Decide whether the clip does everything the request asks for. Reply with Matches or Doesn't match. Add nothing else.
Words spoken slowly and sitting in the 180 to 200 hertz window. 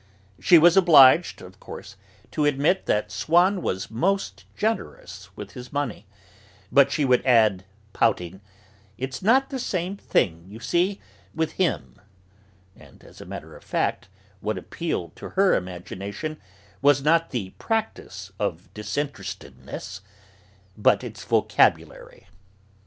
Doesn't match